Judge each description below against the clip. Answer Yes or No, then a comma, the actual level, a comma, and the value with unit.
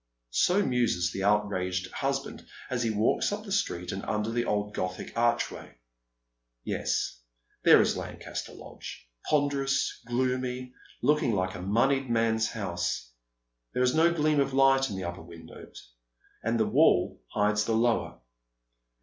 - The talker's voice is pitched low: Yes, low, 115 Hz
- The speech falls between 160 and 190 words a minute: No, average, 145 wpm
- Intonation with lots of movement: Yes, wide, 5.7 semitones